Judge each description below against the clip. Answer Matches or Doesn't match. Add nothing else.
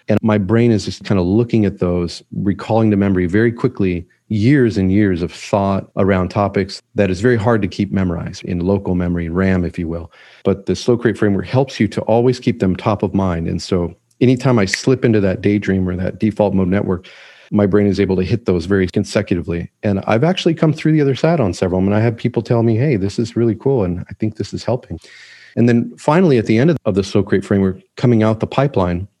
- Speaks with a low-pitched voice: Matches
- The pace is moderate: Doesn't match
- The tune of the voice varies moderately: Matches